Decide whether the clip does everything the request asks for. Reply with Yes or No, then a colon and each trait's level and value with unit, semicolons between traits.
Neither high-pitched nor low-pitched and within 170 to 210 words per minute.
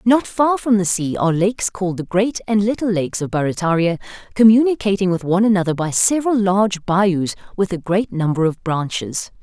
No: high, 195 Hz; average, 185 wpm